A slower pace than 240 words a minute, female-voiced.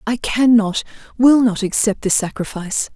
Yes: average, 140 wpm; female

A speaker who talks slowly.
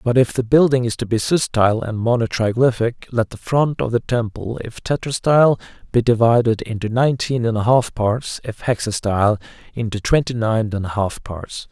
No: average, 180 wpm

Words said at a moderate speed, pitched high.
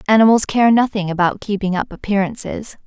Yes: average, 145 wpm; high, 205 Hz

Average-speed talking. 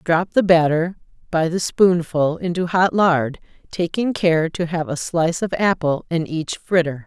Yes: average, 170 wpm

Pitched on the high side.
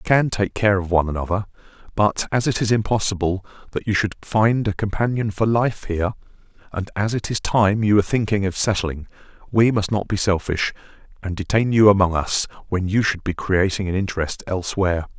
No: low, 100 Hz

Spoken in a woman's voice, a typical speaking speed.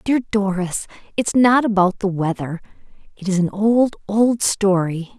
Yes: female; average, 160 wpm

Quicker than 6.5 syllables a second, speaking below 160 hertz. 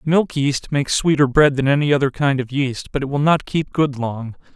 No: 5.1 syllables/s; medium, 140 Hz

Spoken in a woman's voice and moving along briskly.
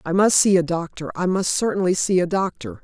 Yes: female; fast, 235 wpm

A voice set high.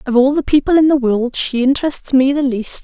Yes: very high, 270 Hz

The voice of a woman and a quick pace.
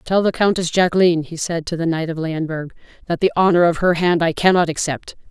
Yes: female; fast, 225 wpm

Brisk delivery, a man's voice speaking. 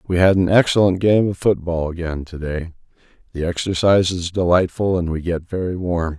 No: average, 175 wpm; male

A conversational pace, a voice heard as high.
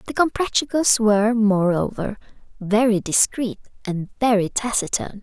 No: slow, 105 wpm; high, 220 Hz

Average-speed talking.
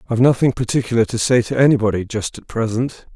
Yes: average, 190 wpm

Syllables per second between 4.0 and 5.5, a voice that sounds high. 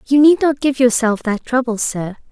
Yes: 4.9 syllables/s; very high, 250 Hz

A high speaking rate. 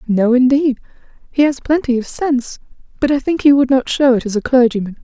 Yes: fast, 215 wpm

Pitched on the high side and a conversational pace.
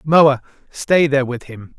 No: medium, 140 Hz; average, 170 wpm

